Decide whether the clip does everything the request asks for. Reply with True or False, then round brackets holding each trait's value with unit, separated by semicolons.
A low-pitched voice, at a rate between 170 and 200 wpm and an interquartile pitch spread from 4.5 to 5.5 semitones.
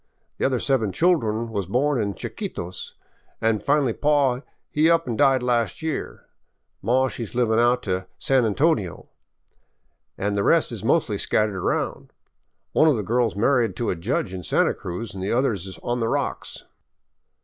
True (115 Hz; 175 wpm; 4.8 semitones)